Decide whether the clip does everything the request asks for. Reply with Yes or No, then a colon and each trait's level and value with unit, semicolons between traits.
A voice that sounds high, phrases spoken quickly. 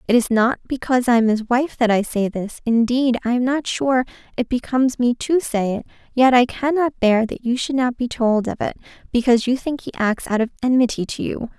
Yes: high, 245 Hz; fast, 230 wpm